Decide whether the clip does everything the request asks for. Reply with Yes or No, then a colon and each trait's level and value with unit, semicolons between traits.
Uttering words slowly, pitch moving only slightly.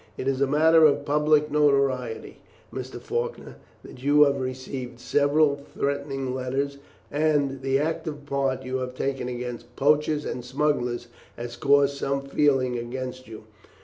No: average, 145 wpm; narrow, 2.3 semitones